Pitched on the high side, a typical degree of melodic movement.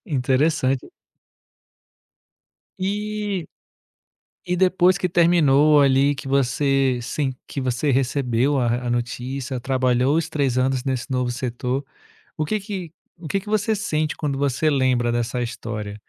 No: low, 135 Hz; average, 4.2 semitones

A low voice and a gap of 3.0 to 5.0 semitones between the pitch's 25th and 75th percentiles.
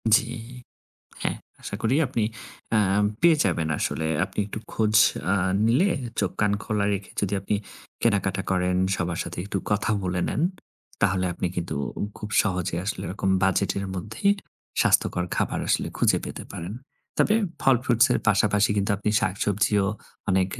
No: low, 100 Hz; narrow, 2.5 semitones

